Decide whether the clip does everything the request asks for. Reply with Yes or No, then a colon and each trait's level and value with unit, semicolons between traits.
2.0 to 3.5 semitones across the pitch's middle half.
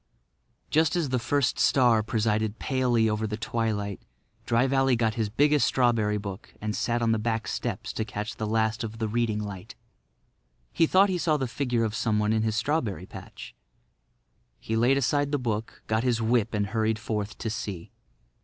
Yes: narrow, 2.6 semitones